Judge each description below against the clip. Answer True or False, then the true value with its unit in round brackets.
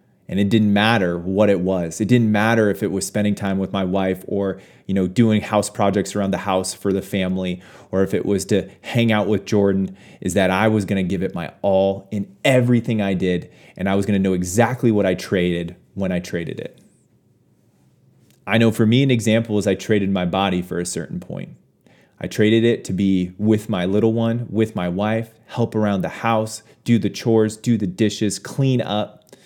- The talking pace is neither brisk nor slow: False (215 wpm)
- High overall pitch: False (100 Hz)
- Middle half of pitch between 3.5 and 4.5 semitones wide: False (2.7 semitones)